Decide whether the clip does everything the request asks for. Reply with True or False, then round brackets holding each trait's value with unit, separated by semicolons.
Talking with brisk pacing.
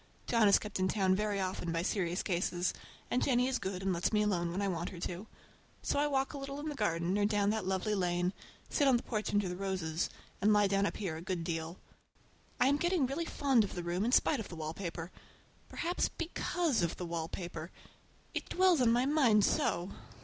True (220 wpm)